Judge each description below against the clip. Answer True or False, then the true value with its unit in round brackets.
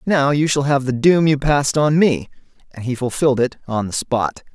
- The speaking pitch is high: False (135 Hz)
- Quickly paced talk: True (225 wpm)